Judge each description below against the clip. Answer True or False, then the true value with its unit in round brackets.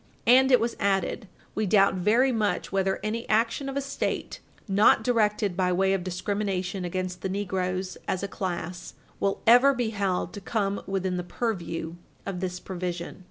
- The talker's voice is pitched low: False (195 Hz)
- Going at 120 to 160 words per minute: False (170 wpm)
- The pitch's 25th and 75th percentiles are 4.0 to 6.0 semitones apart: False (3.2 semitones)